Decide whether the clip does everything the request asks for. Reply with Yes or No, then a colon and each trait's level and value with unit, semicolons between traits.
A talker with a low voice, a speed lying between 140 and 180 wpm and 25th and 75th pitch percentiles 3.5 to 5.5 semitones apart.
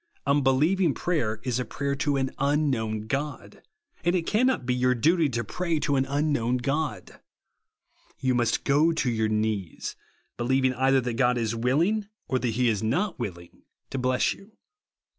Yes: low, 130 Hz; average, 165 wpm; average, 4.0 semitones